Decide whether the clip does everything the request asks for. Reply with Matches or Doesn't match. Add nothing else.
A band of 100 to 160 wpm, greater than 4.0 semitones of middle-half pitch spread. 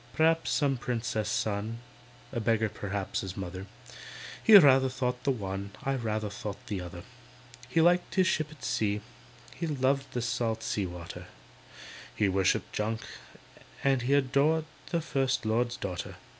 Matches